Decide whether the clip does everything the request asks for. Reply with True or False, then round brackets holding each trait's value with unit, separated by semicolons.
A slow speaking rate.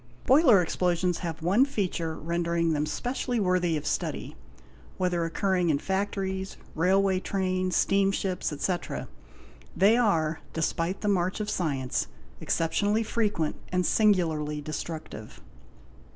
True (120 wpm)